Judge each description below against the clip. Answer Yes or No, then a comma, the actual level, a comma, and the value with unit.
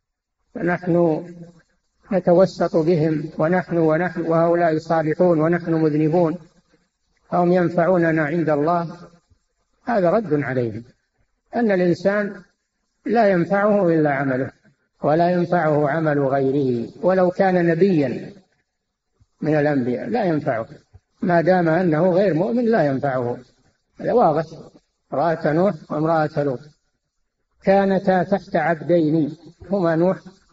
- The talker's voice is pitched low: No, medium, 170 Hz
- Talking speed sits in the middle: Yes, average, 100 wpm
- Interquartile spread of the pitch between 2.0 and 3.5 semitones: Yes, average, 2.9 semitones